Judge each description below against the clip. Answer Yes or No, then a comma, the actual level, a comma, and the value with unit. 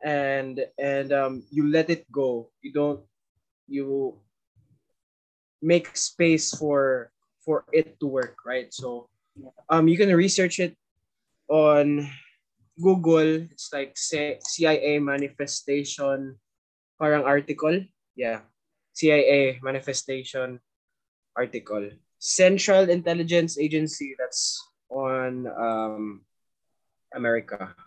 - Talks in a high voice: No, medium, 140 Hz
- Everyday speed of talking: No, slow, 95 wpm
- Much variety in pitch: No, average, 3.7 semitones